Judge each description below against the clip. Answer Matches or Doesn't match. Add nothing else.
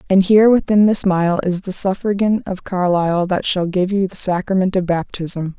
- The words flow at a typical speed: Matches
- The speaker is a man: Doesn't match